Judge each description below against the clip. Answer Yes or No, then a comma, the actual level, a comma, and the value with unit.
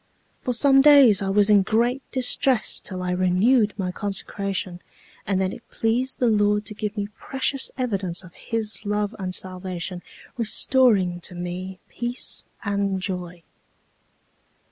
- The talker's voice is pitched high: Yes, high, 205 Hz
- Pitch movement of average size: Yes, average, 4.0 semitones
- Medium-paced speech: Yes, average, 145 wpm